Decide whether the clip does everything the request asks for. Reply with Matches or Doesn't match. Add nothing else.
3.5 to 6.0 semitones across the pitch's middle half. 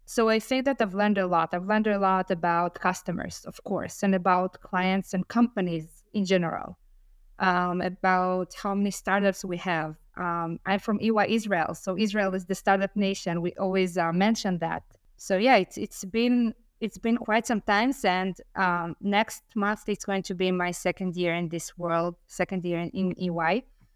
Doesn't match